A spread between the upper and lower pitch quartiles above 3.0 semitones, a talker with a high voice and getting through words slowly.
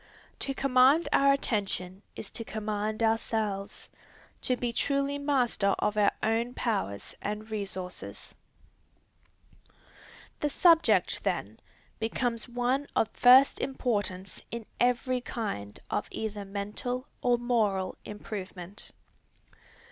Yes: average, 3.7 semitones; high, 225 Hz; slow, 105 wpm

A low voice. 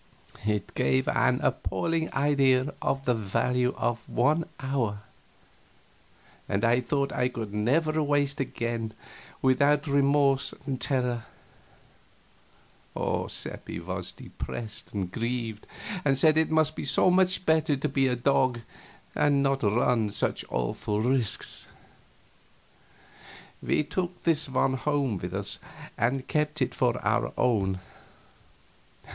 Yes: low, 130 Hz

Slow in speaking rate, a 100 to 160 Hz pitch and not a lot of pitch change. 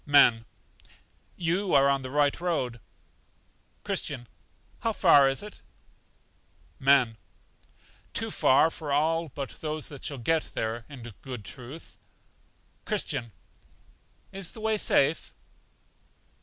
No: slow, 115 wpm; medium, 140 Hz; average, 4.2 semitones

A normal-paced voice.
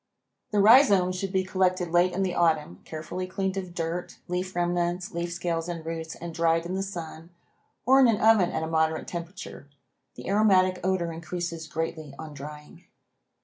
Yes: average, 175 wpm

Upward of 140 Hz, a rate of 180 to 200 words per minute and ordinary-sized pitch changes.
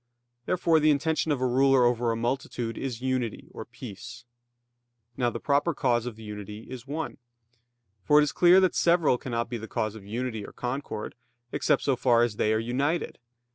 No: low, 125 Hz; average, 185 wpm; average, 3.6 semitones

